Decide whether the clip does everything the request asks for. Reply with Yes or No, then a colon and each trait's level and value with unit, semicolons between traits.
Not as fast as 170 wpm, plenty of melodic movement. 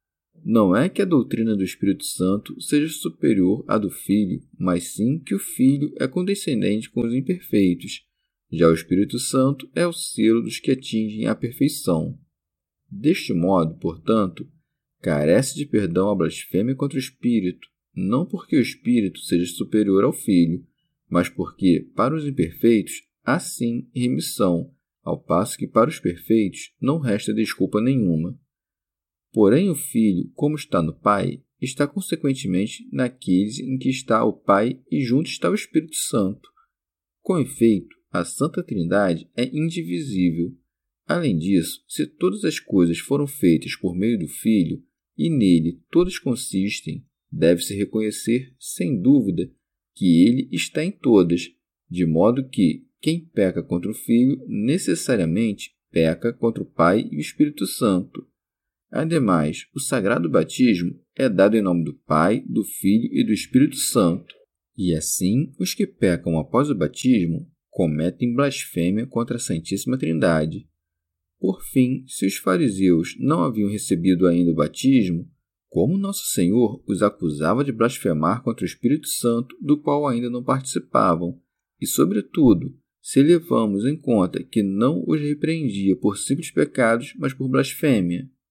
Yes: average, 145 wpm; wide, 7.3 semitones